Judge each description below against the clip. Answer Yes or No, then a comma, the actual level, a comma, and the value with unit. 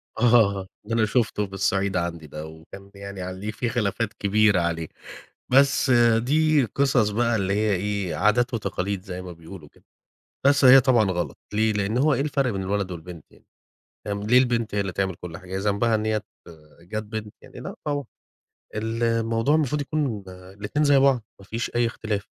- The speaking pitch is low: Yes, low, 105 Hz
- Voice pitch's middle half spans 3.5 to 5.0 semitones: Yes, average, 3.8 semitones